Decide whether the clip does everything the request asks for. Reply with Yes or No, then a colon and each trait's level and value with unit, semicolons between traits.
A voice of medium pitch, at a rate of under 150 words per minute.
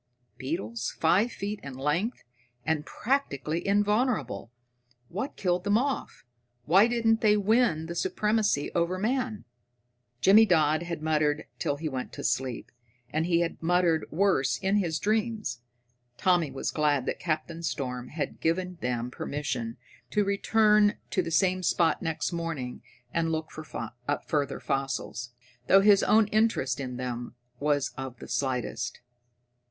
Yes: medium, 165 Hz; average, 140 wpm